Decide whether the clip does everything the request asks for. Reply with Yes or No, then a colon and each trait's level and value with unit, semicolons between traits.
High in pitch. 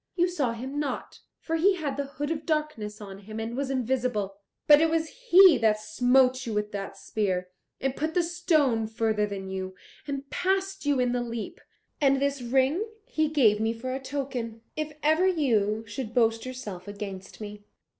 Yes: very high, 255 Hz